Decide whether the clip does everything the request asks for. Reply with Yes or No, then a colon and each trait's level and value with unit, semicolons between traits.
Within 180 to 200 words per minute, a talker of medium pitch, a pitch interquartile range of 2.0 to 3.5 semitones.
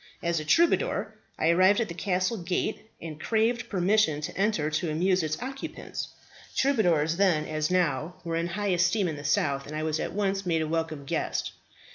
No: average, 190 wpm; medium, 175 Hz; average, 4.1 semitones